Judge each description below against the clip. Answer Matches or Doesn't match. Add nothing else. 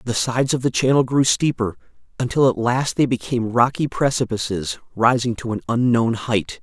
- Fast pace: Doesn't match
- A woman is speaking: Doesn't match